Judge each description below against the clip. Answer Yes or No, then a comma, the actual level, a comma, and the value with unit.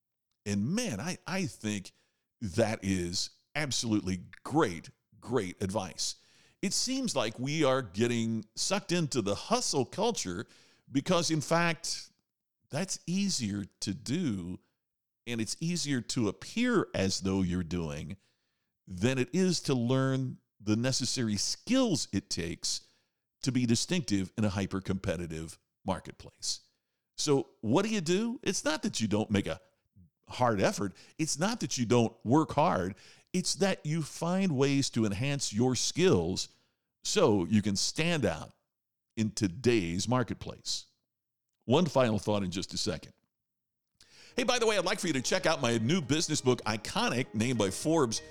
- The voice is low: Yes, low, 120 Hz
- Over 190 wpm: No, average, 150 wpm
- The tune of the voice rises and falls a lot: Yes, wide, 7.4 semitones